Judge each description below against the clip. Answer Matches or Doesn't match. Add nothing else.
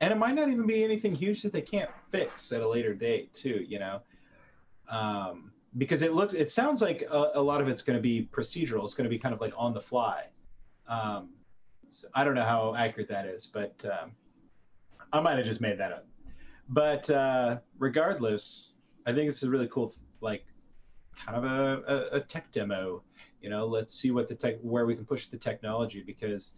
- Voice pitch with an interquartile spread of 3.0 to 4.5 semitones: Doesn't match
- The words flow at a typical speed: Doesn't match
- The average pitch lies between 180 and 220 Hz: Doesn't match